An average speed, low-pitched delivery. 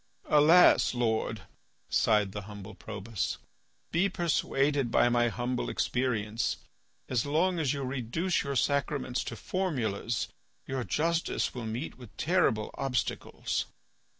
No: slow, 120 wpm; low, 125 Hz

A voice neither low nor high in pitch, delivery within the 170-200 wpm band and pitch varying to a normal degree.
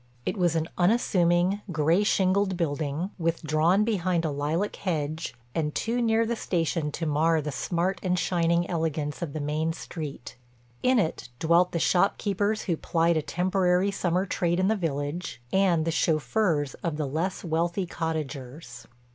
No: medium, 170 Hz; average, 160 wpm; average, 3.1 semitones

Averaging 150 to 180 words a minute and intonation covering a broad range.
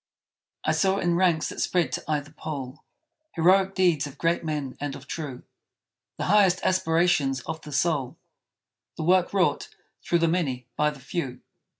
No: average, 165 wpm; average, 3.8 semitones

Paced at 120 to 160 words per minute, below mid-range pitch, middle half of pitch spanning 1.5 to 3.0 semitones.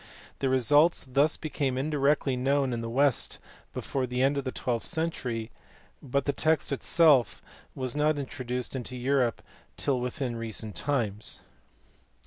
Yes: average, 145 wpm; low, 130 Hz; narrow, 2.6 semitones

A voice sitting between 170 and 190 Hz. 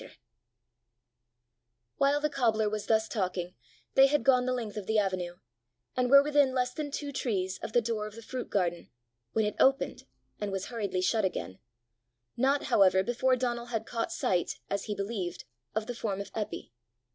No: high, 220 Hz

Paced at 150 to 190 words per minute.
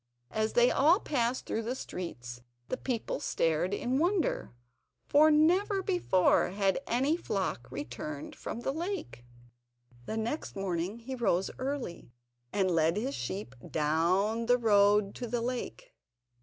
No: average, 140 wpm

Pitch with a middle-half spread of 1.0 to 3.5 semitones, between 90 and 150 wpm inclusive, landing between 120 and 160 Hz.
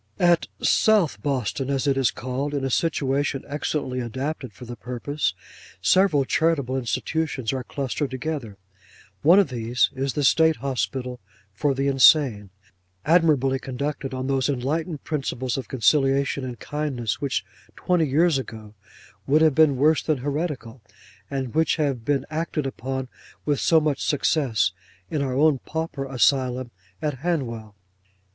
Yes: average, 3.0 semitones; average, 145 wpm; low, 135 Hz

